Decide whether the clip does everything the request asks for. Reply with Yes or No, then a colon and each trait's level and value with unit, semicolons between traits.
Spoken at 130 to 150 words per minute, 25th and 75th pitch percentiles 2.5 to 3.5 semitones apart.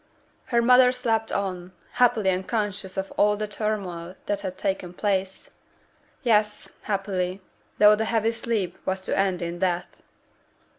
Yes: average, 140 wpm; average, 2.8 semitones